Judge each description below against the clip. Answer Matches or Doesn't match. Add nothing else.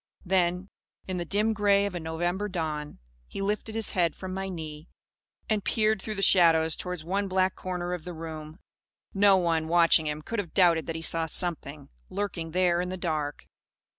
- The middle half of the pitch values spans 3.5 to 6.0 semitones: Doesn't match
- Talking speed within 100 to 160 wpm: Doesn't match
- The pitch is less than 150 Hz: Doesn't match